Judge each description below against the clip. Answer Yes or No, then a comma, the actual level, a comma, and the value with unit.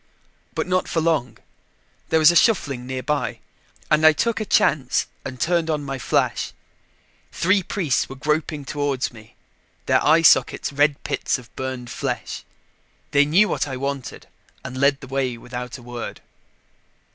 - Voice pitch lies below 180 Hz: Yes, medium, 140 Hz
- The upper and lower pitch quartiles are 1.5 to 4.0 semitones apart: Yes, average, 3.5 semitones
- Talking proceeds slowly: No, average, 155 wpm